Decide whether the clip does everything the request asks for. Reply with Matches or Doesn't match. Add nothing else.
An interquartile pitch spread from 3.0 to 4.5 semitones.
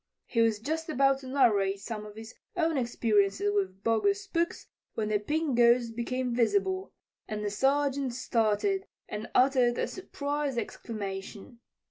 Doesn't match